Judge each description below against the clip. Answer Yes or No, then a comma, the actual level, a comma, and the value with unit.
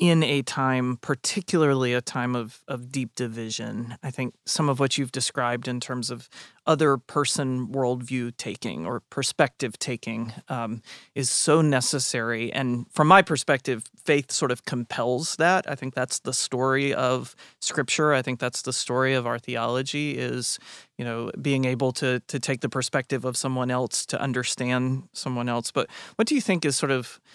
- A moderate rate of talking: Yes, average, 175 wpm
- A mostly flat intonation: Yes, narrow, 2.3 semitones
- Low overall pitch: Yes, low, 130 Hz